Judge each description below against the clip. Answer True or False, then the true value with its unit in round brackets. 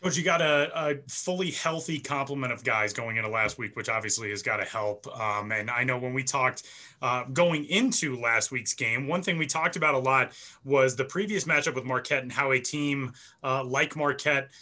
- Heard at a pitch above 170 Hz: False (135 Hz)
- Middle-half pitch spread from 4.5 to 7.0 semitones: False (3.4 semitones)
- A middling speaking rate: False (220 wpm)